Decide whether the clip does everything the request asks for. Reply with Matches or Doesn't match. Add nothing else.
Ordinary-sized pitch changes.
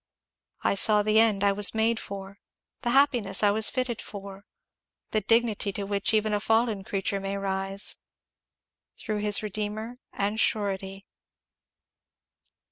Doesn't match